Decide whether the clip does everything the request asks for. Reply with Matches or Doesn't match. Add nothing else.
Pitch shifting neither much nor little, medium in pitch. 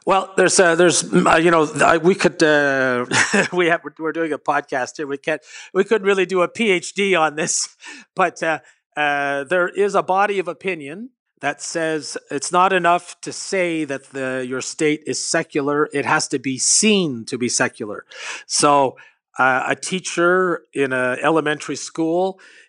Matches